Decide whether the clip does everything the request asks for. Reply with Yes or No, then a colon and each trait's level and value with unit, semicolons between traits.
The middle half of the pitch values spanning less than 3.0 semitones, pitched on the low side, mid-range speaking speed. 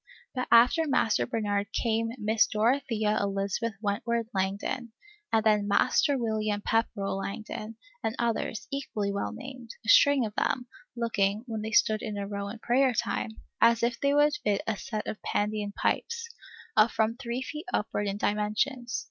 No: narrow, 2.4 semitones; high, 220 Hz; average, 165 wpm